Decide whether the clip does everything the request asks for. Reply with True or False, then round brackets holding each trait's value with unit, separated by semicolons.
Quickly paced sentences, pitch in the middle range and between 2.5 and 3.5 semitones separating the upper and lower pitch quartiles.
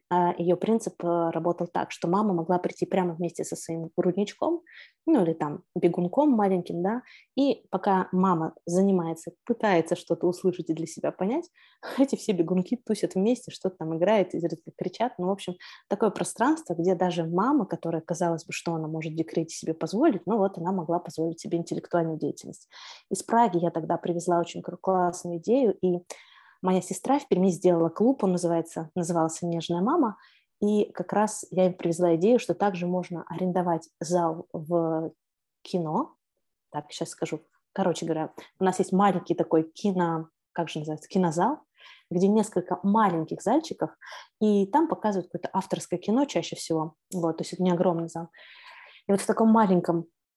True (165 wpm; 180 Hz; 2.9 semitones)